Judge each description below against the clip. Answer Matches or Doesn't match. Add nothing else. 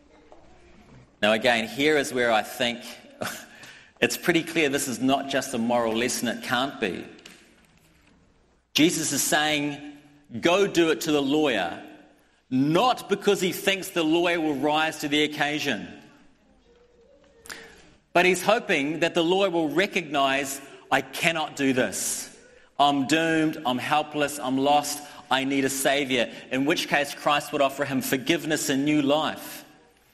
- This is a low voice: Doesn't match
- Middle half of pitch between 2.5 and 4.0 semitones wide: Matches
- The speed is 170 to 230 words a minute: Doesn't match